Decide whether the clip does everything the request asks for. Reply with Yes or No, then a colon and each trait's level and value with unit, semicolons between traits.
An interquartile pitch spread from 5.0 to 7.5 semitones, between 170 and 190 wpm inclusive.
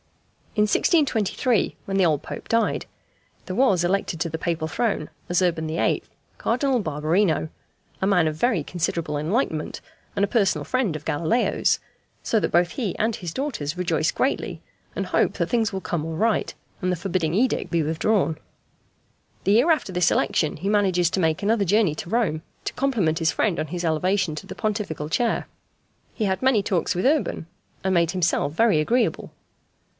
Yes: wide, 5.4 semitones; average, 180 wpm